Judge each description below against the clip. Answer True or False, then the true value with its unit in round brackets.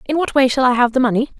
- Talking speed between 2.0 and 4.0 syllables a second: False (7.2 syllables/s)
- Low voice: False (255 Hz)